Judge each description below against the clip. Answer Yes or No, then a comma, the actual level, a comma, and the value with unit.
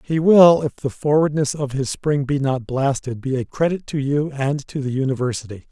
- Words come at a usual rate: No, fast, 210 wpm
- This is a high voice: No, medium, 140 Hz